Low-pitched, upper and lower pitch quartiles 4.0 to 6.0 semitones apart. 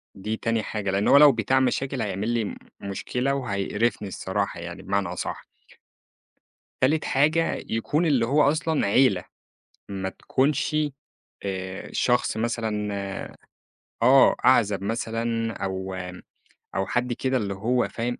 Yes: low, 115 Hz; average, 4.7 semitones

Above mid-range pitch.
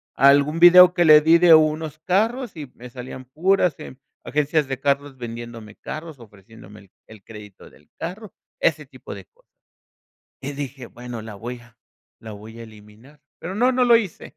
No: medium, 140 Hz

